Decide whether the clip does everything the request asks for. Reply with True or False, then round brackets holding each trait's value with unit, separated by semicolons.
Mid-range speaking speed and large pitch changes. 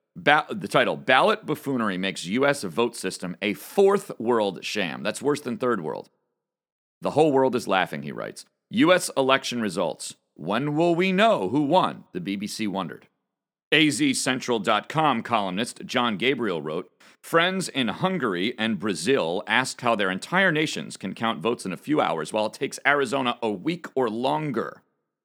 True (160 wpm; 6.3 semitones)